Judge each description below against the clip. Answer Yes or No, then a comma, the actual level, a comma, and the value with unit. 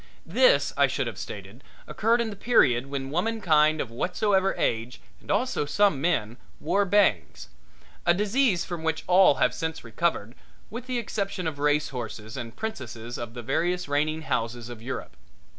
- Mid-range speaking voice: Yes, medium, 160 Hz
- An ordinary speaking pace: Yes, average, 160 wpm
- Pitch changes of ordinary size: No, wide, 8.5 semitones